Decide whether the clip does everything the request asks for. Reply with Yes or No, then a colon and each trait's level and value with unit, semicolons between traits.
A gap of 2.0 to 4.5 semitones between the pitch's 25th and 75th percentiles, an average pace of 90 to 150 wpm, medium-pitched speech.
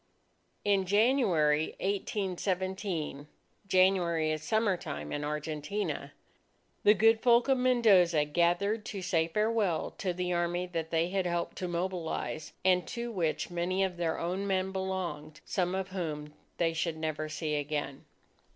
Yes: average, 3.4 semitones; average, 140 wpm; medium, 180 Hz